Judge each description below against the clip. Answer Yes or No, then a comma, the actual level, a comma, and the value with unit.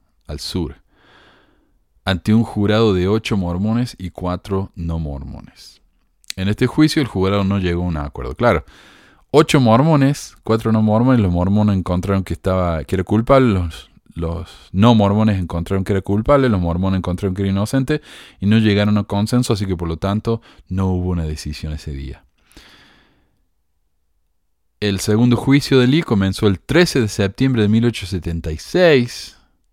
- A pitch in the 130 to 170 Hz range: No, low, 100 Hz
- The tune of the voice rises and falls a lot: No, average, 4.3 semitones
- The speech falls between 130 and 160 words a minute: Yes, average, 155 wpm